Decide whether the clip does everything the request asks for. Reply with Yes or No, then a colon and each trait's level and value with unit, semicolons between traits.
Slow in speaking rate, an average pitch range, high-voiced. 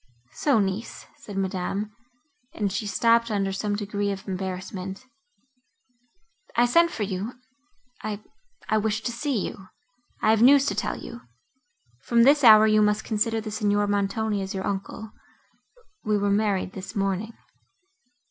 Yes: slow, 130 wpm; average, 3.4 semitones; high, 215 Hz